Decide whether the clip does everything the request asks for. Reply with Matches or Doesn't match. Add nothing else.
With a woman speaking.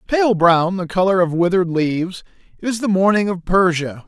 Doesn't match